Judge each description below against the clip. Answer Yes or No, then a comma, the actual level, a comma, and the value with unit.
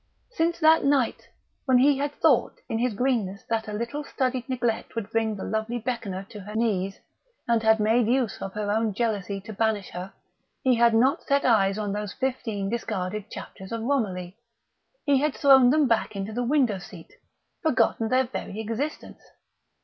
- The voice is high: Yes, high, 225 Hz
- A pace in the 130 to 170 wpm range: No, average, 180 wpm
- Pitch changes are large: No, average, 3.7 semitones